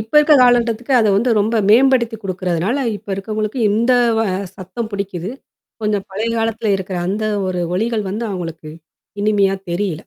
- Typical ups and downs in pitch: Yes, average, 3.3 semitones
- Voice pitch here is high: Yes, high, 210 Hz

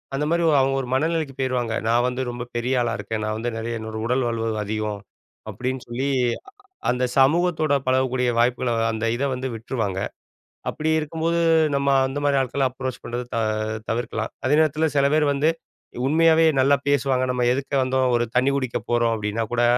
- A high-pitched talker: No, low, 130 Hz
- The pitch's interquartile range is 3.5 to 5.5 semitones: No, average, 2.9 semitones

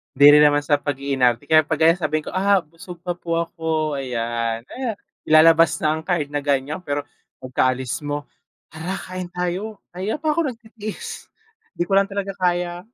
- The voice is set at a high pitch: No, medium, 160 Hz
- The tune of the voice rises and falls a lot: No, average, 4.1 semitones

